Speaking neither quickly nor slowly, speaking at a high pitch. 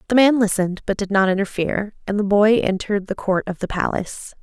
No: fast, 215 wpm; high, 200 Hz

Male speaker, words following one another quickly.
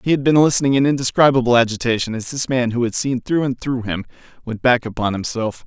Yes: male; fast, 220 wpm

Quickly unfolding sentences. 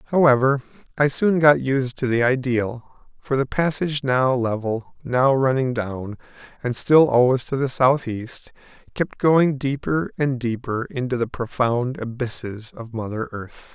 No: average, 150 wpm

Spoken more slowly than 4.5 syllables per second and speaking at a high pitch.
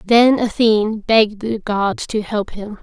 Yes: 4.1 syllables/s; high, 215 Hz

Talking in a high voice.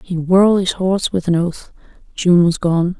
No: medium, 180 Hz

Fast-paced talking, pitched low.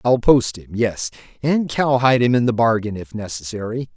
No: average, 165 wpm; low, 115 Hz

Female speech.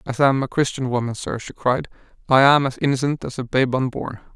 No: male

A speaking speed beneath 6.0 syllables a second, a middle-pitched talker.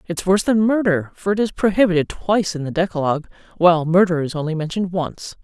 No: 6.5 syllables/s; medium, 180 Hz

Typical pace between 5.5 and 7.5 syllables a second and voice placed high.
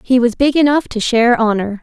Yes: 5.8 syllables/s; high, 245 Hz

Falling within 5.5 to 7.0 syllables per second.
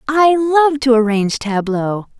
No: 4.1 syllables/s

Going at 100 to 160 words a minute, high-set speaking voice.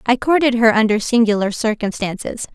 Yes: average, 140 wpm; high, 230 Hz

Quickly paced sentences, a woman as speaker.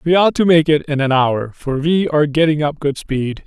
No: fast, 260 wpm; male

